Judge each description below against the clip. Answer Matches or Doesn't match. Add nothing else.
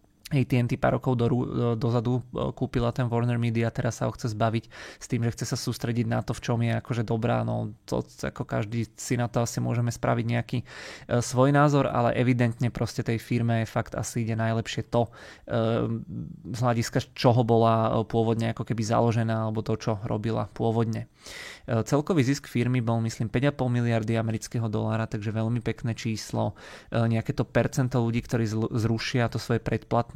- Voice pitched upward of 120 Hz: Doesn't match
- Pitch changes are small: Matches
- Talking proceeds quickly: Matches